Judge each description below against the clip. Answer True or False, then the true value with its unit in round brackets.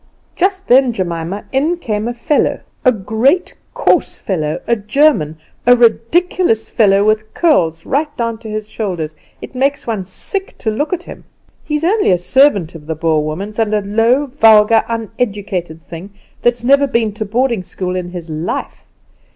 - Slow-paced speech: False (165 wpm)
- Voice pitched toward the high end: True (220 Hz)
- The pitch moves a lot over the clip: True (6.2 semitones)